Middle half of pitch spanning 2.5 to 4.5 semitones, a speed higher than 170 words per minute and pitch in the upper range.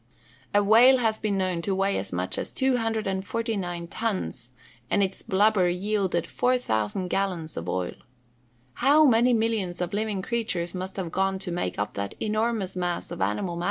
No: average, 4.0 semitones; average, 165 wpm; high, 195 Hz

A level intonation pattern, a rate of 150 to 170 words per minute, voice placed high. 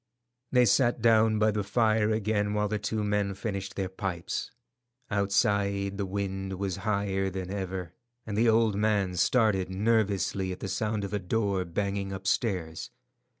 No: narrow, 1.9 semitones; average, 155 wpm; low, 100 Hz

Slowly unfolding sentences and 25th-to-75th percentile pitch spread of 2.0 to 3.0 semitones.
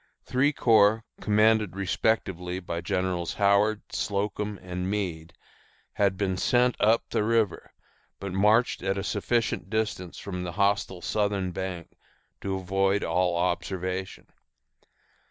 Yes: slow, 120 wpm; narrow, 2.5 semitones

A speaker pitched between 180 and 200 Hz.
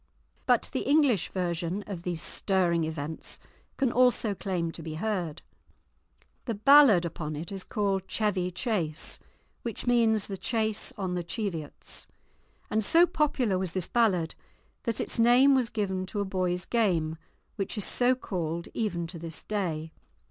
Yes: high, 190 Hz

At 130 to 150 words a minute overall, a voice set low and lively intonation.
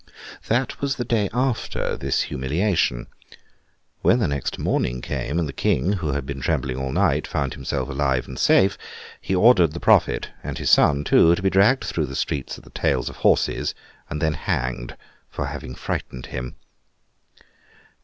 No: average, 165 wpm; very low, 75 Hz; wide, 6.7 semitones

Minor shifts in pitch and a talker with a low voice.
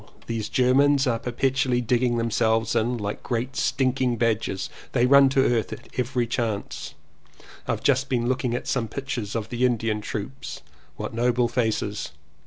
Yes: narrow, 2.2 semitones; low, 120 Hz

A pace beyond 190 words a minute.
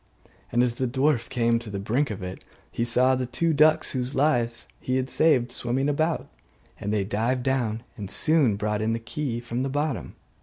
Yes: average, 200 wpm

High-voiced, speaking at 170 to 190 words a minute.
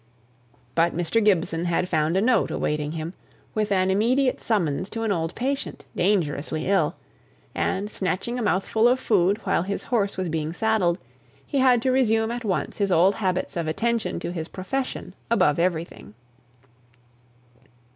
No: high, 195 Hz; average, 155 wpm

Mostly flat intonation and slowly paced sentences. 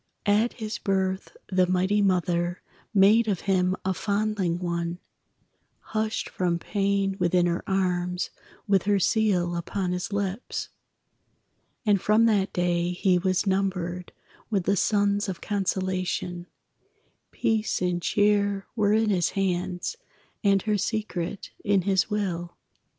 Yes: narrow, 2.3 semitones; slow, 130 wpm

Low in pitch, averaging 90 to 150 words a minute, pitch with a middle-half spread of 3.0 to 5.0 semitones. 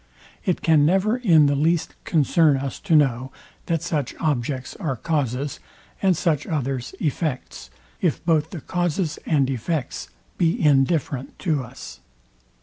No: medium, 150 Hz; average, 140 wpm; average, 3.7 semitones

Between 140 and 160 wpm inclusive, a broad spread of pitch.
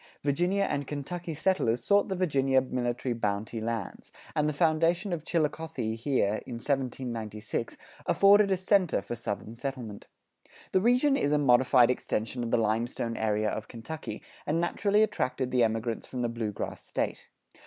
Yes: average, 155 wpm; wide, 6.3 semitones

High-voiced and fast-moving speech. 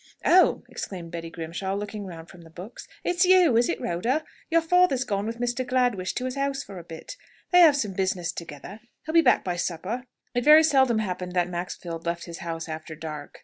Yes: high, 195 Hz; fast, 215 wpm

